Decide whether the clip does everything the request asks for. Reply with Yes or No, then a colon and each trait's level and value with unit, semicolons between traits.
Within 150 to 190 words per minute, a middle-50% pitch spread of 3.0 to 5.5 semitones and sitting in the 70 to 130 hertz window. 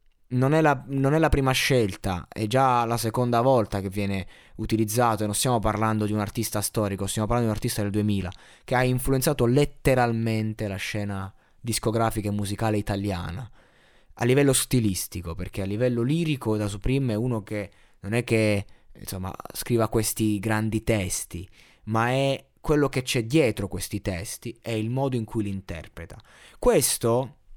Yes: fast, 170 wpm; average, 3.4 semitones; low, 110 Hz